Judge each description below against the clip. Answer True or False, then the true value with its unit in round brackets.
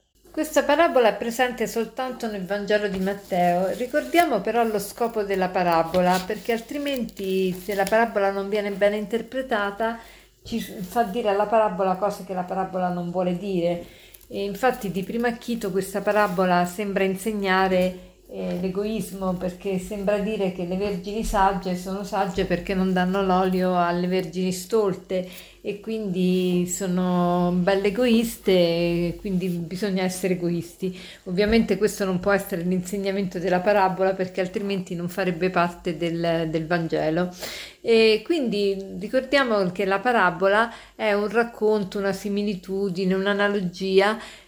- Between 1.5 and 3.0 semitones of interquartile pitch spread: True (2.6 semitones)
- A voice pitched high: True (195 Hz)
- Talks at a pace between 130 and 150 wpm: True (135 wpm)